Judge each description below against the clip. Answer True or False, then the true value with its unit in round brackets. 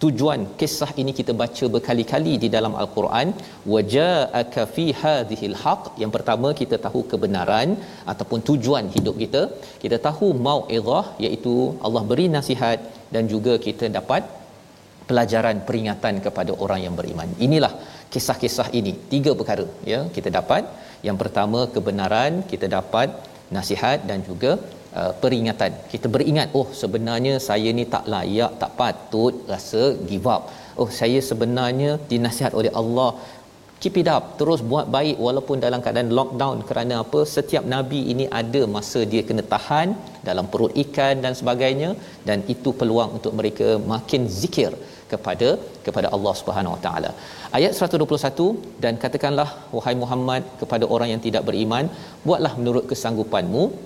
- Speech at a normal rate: False (140 wpm)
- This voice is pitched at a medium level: False (125 Hz)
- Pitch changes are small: False (4.3 semitones)